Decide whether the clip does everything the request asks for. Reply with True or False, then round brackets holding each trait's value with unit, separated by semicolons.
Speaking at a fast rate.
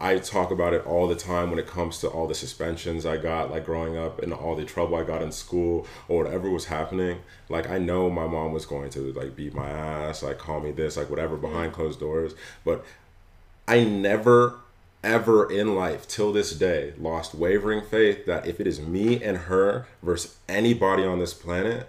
True (210 wpm)